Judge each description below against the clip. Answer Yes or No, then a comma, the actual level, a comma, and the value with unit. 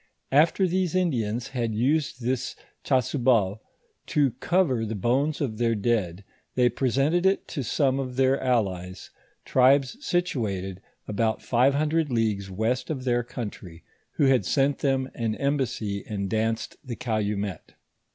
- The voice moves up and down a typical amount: Yes, average, 4.3 semitones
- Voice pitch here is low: Yes, low, 125 Hz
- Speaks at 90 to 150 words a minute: Yes, average, 140 wpm